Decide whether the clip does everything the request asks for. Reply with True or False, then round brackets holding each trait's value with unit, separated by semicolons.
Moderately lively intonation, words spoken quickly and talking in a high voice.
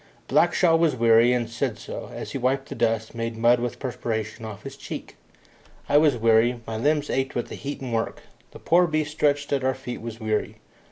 False (3.9 semitones; 210 wpm; 120 Hz)